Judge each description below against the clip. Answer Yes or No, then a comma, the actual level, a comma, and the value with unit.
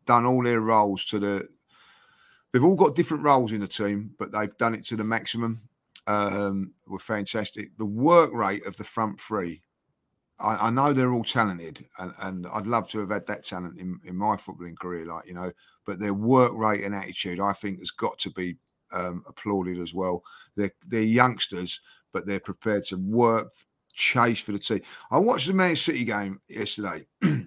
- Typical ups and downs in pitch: Yes, average, 3.2 semitones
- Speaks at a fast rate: No, average, 195 wpm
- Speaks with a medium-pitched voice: No, low, 105 Hz